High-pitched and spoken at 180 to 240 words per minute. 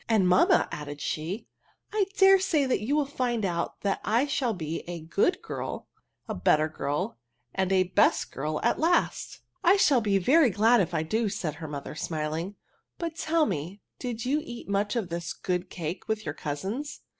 Yes: high, 200 Hz; average, 200 wpm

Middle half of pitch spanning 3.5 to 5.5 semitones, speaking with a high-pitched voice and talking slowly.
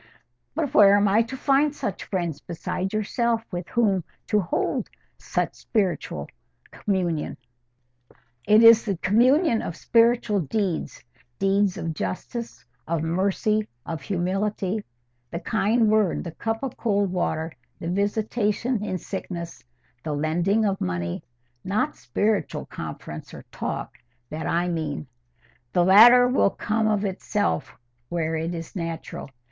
Yes: average, 4.8 semitones; high, 195 Hz; slow, 125 wpm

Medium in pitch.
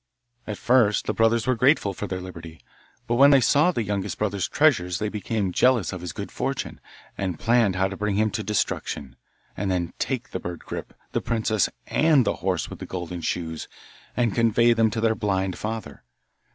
No: low, 105 Hz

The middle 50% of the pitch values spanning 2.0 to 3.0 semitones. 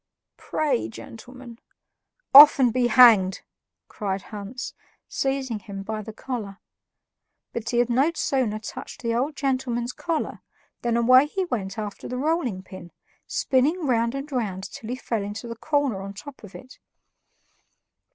No: average, 4.2 semitones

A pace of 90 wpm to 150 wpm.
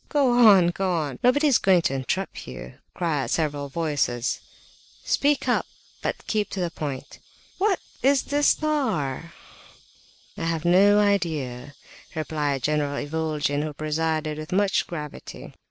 Yes: average, 140 wpm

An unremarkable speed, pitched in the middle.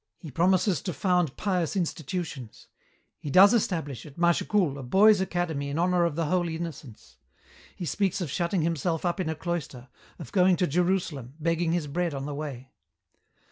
Yes: average, 175 wpm; medium, 170 Hz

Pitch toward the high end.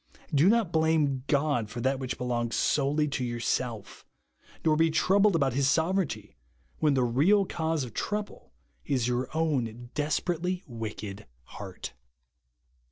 No: medium, 140 Hz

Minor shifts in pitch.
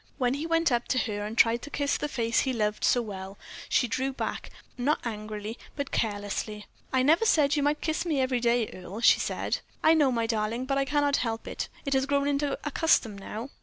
No: average, 4.3 semitones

